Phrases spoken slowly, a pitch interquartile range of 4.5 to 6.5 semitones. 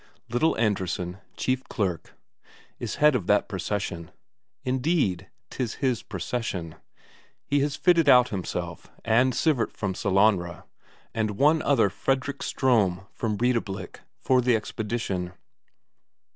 Yes: slow, 115 wpm; wide, 5.4 semitones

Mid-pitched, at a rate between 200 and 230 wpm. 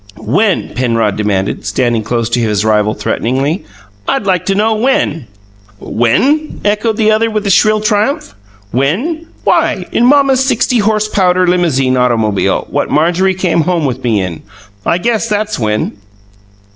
No: medium, 175 Hz; average, 150 wpm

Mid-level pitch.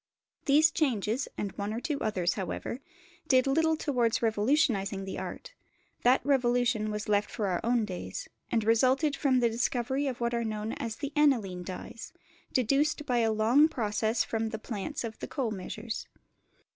No: high, 235 Hz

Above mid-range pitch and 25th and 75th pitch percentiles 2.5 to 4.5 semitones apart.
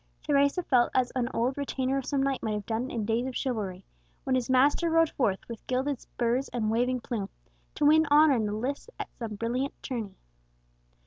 Yes: very high, 255 Hz; average, 3.2 semitones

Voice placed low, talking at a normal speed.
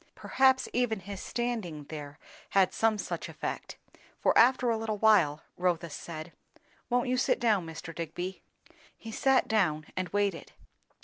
No: high, 200 Hz; average, 145 wpm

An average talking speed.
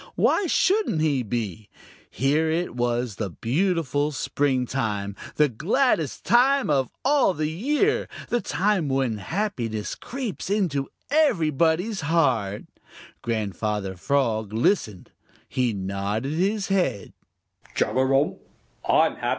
No: slow, 100 wpm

